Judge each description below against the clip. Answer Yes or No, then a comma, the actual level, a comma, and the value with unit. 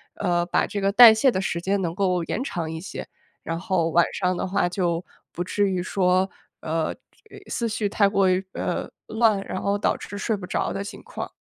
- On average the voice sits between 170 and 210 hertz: Yes, high, 190 Hz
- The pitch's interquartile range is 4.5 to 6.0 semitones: No, narrow, 2.5 semitones